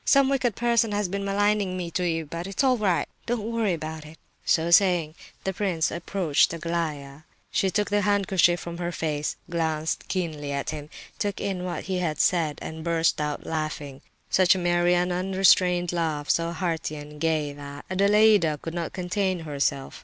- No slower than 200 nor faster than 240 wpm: No, average, 175 wpm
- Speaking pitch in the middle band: Yes, medium, 175 Hz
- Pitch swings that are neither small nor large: Yes, average, 3.5 semitones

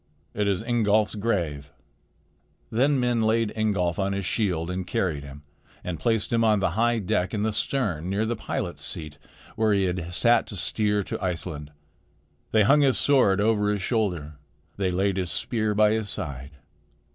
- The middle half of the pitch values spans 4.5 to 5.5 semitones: No, average, 3.9 semitones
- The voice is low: Yes, low, 100 Hz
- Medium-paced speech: Yes, average, 175 wpm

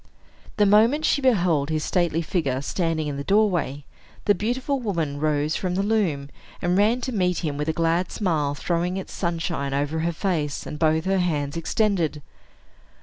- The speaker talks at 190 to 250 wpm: No, average, 175 wpm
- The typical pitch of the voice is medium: Yes, medium, 170 Hz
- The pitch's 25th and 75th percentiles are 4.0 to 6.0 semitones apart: Yes, average, 4.7 semitones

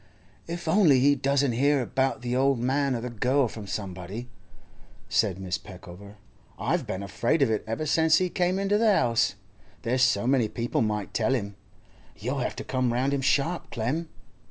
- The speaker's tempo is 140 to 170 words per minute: No, average, 180 wpm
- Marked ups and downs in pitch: No, average, 4.5 semitones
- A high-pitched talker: No, low, 125 Hz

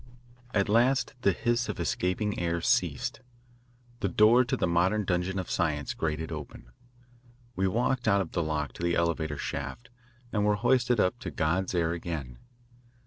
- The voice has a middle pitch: No, very low, 90 Hz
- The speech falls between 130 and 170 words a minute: Yes, average, 165 wpm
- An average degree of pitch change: Yes, average, 4.4 semitones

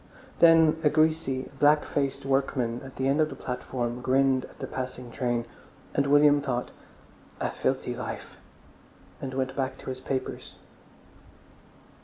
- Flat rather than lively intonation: Yes, narrow, 2.1 semitones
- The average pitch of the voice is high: No, low, 135 Hz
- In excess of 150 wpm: No, average, 145 wpm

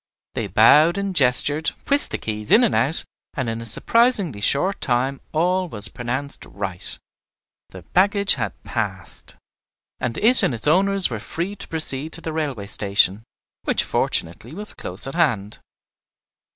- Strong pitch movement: Yes, wide, 8.6 semitones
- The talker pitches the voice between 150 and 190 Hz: No, medium, 140 Hz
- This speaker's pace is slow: No, average, 155 wpm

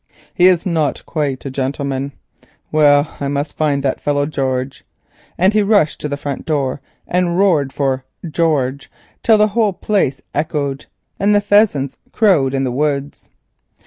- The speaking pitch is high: No, medium, 145 Hz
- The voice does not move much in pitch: No, average, 4.5 semitones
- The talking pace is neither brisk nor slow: Yes, average, 155 wpm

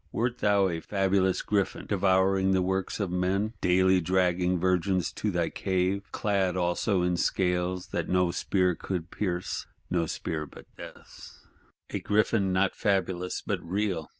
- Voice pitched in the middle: No, very low, 95 Hz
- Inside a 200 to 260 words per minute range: No, average, 145 wpm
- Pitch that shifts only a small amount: Yes, narrow, 1.6 semitones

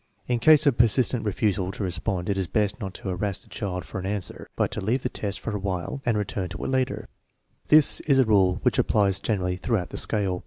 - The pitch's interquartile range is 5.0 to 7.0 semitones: No, average, 4.0 semitones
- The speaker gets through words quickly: Yes, fast, 235 wpm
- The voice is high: No, low, 105 Hz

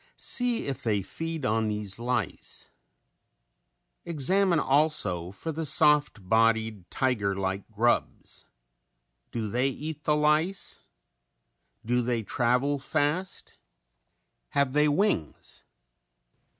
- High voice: No, low, 130 Hz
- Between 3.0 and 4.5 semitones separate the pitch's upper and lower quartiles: No, wide, 5.5 semitones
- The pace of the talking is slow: Yes, slow, 100 wpm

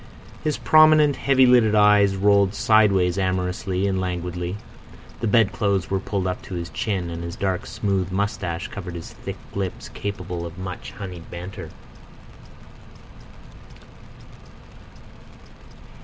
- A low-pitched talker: Yes, very low, 95 Hz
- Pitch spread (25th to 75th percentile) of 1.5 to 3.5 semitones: Yes, narrow, 2.5 semitones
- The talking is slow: Yes, slow, 120 wpm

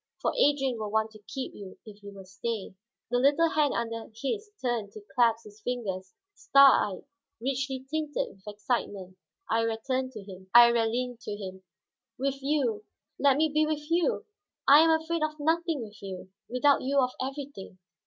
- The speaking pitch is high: Yes, high, 245 Hz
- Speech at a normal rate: Yes, average, 165 wpm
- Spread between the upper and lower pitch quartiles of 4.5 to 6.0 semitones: Yes, wide, 5.4 semitones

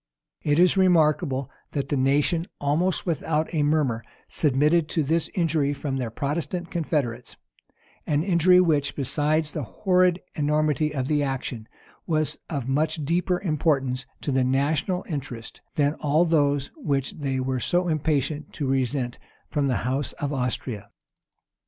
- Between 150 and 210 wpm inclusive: No, average, 140 wpm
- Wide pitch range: No, average, 3.1 semitones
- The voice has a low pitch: No, medium, 145 Hz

